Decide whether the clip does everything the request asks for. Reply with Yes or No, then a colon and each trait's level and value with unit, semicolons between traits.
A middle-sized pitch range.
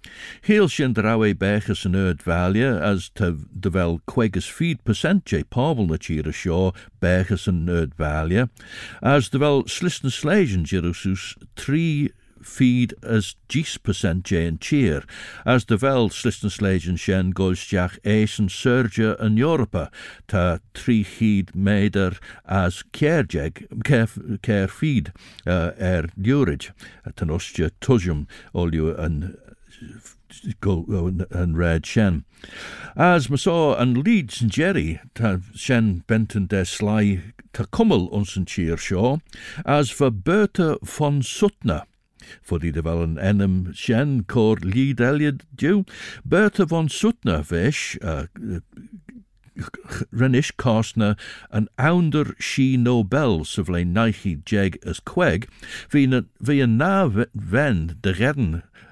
No: wide, 6.1 semitones